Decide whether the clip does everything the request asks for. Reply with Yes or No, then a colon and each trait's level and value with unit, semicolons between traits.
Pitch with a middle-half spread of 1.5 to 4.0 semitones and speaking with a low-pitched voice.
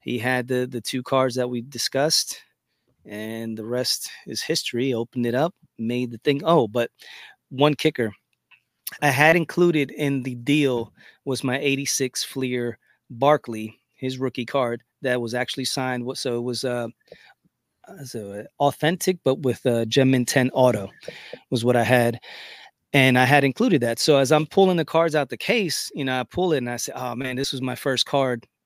Yes: average, 2.8 semitones; low, 130 Hz